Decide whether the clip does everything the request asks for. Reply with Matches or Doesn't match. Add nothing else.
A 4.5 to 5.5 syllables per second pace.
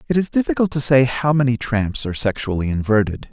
Doesn't match